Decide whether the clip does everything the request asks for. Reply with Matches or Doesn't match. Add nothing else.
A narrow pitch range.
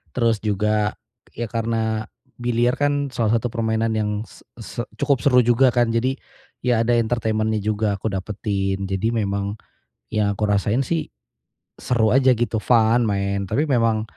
Matches